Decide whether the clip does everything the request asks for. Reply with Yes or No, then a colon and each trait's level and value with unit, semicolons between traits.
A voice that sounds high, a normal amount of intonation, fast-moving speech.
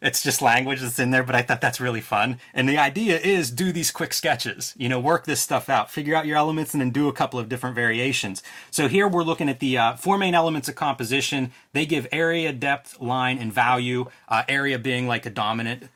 No: low, 135 Hz; average, 3.4 semitones; fast, 235 wpm